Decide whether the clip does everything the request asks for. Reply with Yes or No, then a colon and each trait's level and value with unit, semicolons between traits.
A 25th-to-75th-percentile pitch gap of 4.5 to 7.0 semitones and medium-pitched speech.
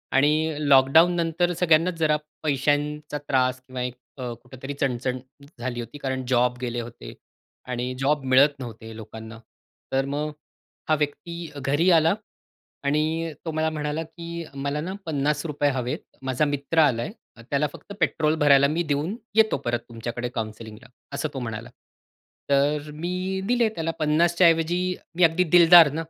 No: average, 4.1 semitones; medium, 150 Hz